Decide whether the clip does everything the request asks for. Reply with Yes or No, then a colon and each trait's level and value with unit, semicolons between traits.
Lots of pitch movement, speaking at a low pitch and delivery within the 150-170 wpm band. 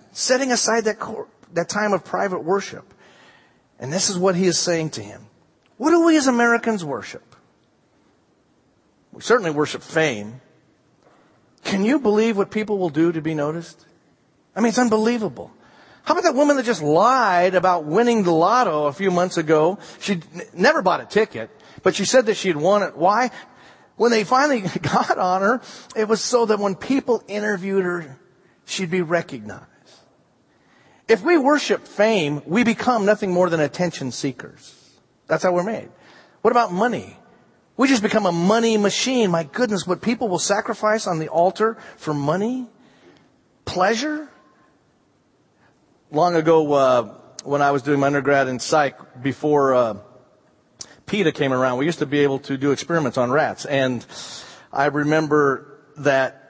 No: wide, 6.7 semitones; medium, 185 Hz; average, 165 wpm